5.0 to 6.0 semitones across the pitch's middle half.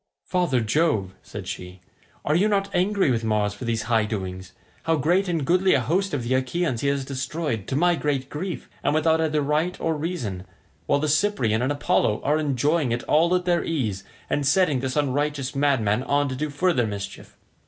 Yes: wide, 5.5 semitones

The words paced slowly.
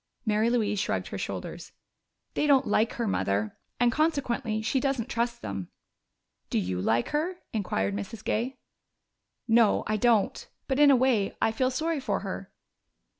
No: average, 160 wpm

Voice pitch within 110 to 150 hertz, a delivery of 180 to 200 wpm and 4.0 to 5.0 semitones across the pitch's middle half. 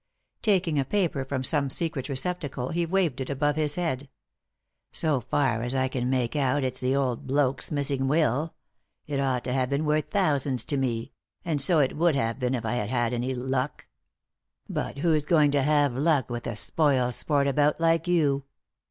No: medium, 140 Hz; average, 195 wpm; average, 3.0 semitones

